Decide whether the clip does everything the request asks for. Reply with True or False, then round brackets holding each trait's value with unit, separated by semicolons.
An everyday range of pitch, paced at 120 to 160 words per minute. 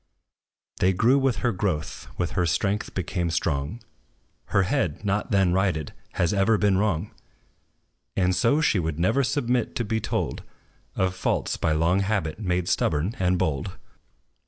True (3.9 semitones; 155 wpm)